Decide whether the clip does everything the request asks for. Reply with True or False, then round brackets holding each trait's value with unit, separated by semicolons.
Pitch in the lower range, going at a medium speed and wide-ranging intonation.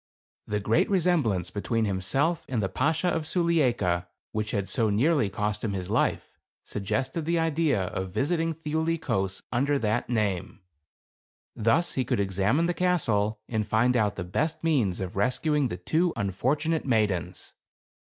True (115 Hz; 155 wpm; 7.9 semitones)